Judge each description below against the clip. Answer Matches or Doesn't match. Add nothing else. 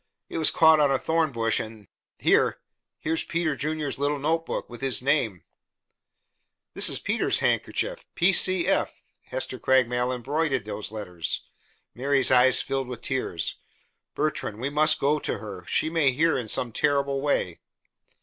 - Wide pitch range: Doesn't match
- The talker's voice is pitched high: Doesn't match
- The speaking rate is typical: Matches